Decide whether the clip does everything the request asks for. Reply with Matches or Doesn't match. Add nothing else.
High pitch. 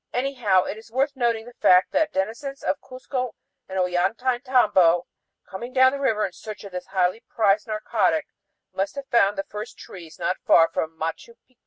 Matches